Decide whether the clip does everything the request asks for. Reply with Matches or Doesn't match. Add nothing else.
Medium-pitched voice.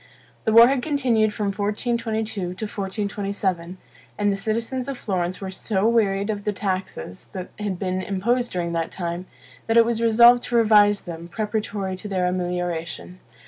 Doesn't match